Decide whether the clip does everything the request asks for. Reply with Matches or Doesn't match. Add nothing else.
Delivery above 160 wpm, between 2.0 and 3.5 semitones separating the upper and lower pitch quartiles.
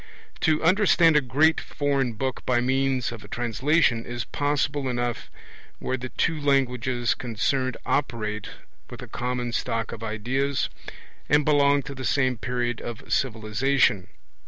Doesn't match